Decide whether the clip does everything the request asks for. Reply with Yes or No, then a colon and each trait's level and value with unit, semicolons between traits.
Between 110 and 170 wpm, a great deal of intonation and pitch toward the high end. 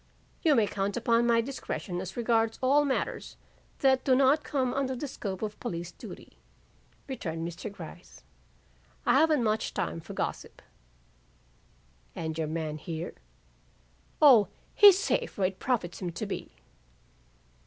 Yes: average, 145 wpm; wide, 7.0 semitones; high, 225 Hz